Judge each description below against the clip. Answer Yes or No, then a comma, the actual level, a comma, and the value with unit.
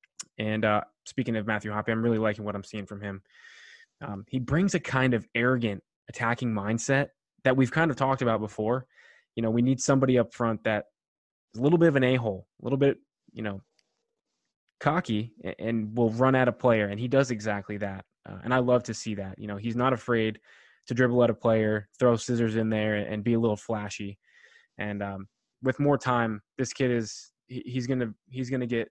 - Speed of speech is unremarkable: No, fast, 210 wpm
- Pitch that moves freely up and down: No, average, 3.3 semitones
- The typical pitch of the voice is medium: No, low, 115 Hz